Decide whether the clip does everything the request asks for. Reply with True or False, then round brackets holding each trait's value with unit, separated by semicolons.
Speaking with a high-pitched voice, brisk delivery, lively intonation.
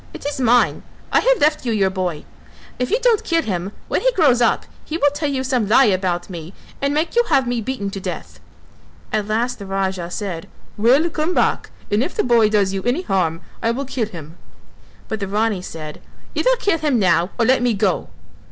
True (225 Hz; 215 wpm; 6.5 semitones)